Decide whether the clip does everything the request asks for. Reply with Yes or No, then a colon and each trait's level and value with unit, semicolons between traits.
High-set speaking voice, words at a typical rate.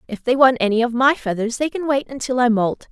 No: high, 245 Hz; fast, 270 wpm